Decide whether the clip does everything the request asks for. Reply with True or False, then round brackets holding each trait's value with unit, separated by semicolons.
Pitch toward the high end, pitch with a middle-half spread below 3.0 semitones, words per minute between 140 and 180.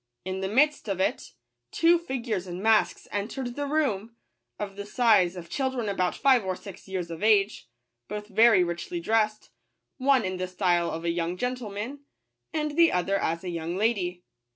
False (205 Hz; 5.4 semitones; 175 wpm)